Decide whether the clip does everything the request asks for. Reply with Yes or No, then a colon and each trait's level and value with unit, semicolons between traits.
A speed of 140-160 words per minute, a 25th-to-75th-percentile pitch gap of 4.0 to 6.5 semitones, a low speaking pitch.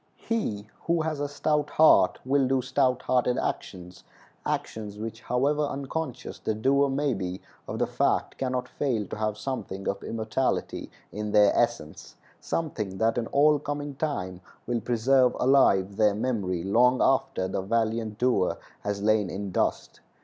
Yes: average, 150 wpm; average, 4.9 semitones; low, 120 Hz